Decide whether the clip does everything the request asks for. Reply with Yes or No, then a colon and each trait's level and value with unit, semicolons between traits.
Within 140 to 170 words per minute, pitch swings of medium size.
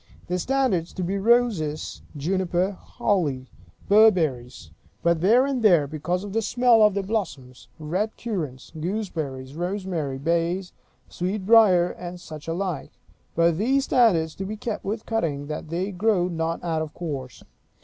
Yes: average, 145 wpm; average, 4.9 semitones